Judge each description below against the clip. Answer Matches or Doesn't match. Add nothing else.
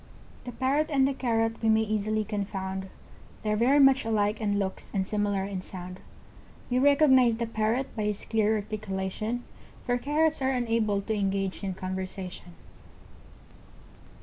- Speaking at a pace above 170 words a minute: Doesn't match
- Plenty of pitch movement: Doesn't match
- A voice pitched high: Matches